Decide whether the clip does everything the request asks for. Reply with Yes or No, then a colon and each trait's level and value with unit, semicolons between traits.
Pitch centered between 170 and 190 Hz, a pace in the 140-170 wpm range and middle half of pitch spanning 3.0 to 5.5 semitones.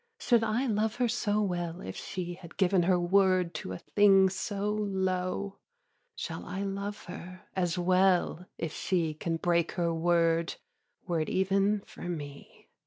No: medium, 185 Hz; average, 160 wpm; narrow, 2.5 semitones